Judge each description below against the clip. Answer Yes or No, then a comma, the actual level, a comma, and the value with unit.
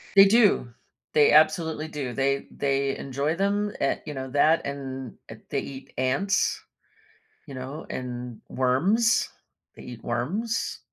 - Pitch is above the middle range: No, medium, 140 Hz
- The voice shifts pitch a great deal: No, average, 4.4 semitones